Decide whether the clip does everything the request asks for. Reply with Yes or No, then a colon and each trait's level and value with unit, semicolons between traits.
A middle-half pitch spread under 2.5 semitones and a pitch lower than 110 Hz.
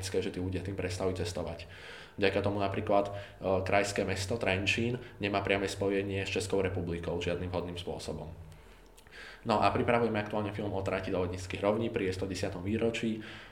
Yes: narrow, 1.9 semitones; very low, 95 Hz